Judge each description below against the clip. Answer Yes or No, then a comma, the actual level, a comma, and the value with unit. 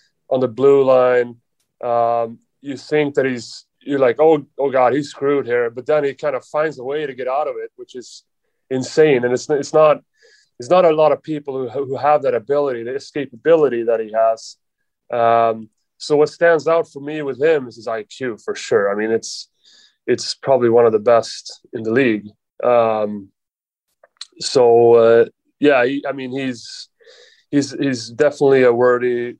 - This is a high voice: No, low, 135 Hz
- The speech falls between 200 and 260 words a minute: No, average, 185 wpm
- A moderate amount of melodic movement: Yes, average, 4.7 semitones